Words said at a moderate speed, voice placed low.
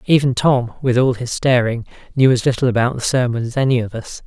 No: fast, 225 wpm; low, 125 Hz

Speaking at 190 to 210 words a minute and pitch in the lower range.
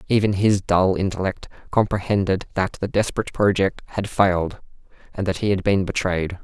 No: average, 160 wpm; very low, 95 Hz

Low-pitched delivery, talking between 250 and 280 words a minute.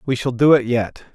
Yes: low, 125 Hz; fast, 260 wpm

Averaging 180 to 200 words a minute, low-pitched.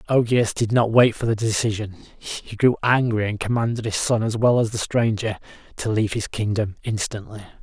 Yes: average, 190 wpm; low, 110 Hz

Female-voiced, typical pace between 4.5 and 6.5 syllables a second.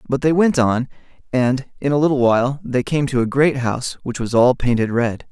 No: male; 5.3 syllables/s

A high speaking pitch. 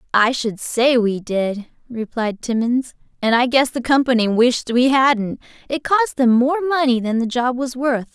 Yes: high, 245 Hz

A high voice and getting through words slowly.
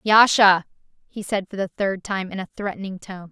No: high, 195 Hz; average, 200 wpm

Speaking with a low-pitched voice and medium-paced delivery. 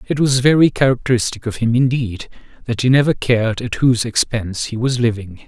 Yes: low, 120 Hz; average, 185 wpm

